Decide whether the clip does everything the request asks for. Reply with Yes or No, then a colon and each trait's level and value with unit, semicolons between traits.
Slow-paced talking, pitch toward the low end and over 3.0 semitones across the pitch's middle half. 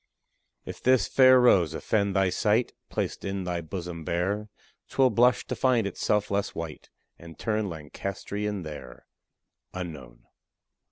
Yes: slow, 130 wpm; low, 100 Hz; average, 4.1 semitones